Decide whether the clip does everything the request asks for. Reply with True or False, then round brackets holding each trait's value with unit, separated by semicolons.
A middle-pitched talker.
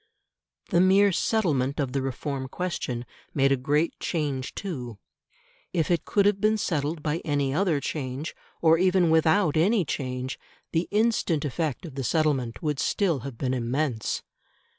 True (150 Hz)